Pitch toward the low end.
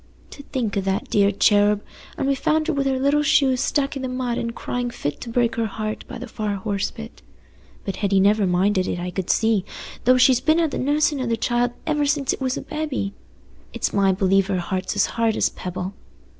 No: high, 230 Hz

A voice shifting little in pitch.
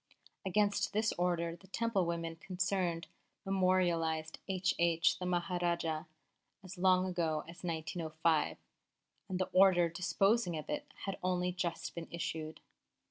Yes: narrow, 2.1 semitones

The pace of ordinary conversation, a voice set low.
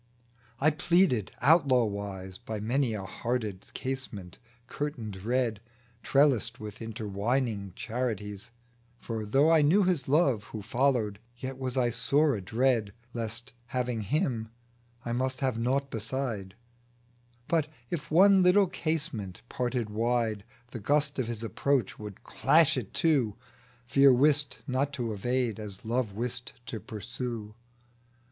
No: slow, 130 wpm; low, 120 Hz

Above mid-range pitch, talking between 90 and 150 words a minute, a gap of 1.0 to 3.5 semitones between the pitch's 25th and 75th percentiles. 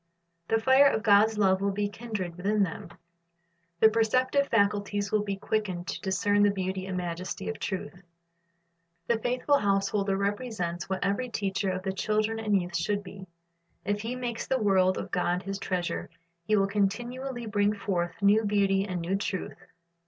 No: high, 200 Hz; average, 175 wpm; narrow, 2.4 semitones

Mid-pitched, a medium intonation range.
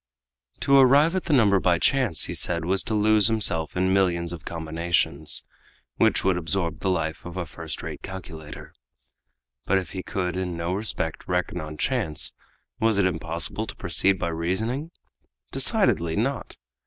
No: very low, 90 Hz; average, 4.0 semitones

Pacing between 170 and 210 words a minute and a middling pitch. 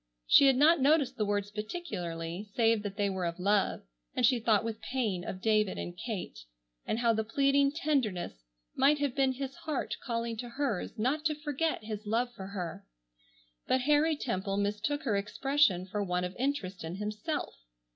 No: average, 180 wpm; high, 225 Hz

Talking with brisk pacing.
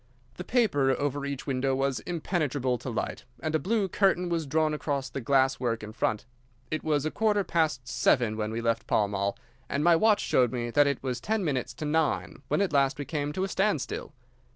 Yes: fast, 215 wpm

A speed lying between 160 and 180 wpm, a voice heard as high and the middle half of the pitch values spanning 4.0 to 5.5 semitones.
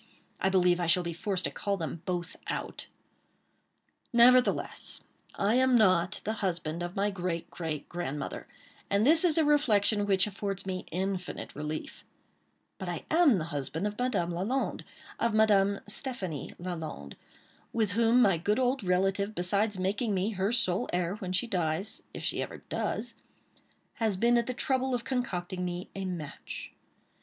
No: average, 150 wpm; high, 195 Hz; average, 4.3 semitones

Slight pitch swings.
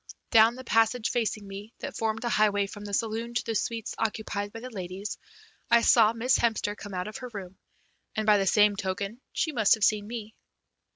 Yes: narrow, 2.1 semitones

